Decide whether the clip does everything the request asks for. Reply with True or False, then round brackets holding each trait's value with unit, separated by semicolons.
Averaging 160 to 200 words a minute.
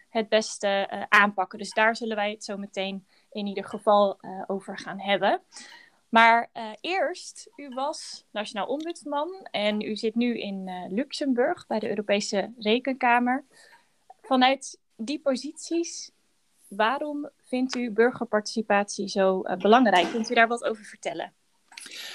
False (140 wpm)